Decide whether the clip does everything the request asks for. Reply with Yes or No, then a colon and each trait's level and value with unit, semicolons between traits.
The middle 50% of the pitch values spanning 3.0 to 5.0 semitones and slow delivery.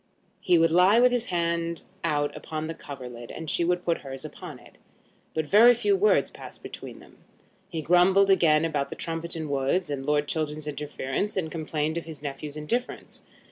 No: average, 3.3 semitones; average, 180 wpm